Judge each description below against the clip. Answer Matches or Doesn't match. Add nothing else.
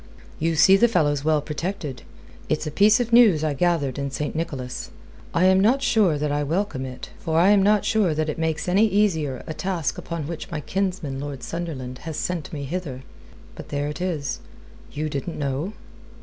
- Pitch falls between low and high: Matches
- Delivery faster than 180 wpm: Matches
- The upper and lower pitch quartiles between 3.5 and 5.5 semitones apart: Matches